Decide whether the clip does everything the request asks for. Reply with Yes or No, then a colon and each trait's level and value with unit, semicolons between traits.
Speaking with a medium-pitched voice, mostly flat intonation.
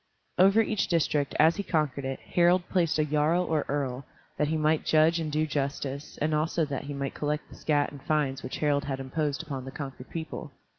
Yes: medium, 150 Hz; narrow, 2.3 semitones